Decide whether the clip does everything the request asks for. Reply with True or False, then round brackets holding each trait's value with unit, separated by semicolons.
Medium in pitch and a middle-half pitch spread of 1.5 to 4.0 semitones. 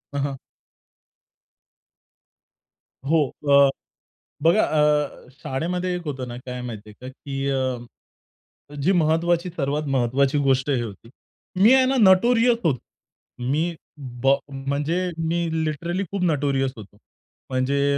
False (145 Hz; 4.5 semitones)